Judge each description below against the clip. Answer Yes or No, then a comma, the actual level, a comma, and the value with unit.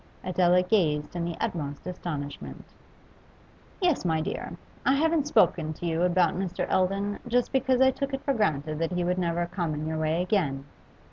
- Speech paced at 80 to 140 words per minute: No, average, 180 wpm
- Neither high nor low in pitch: Yes, medium, 180 Hz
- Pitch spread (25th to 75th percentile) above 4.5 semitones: Yes, average, 4.9 semitones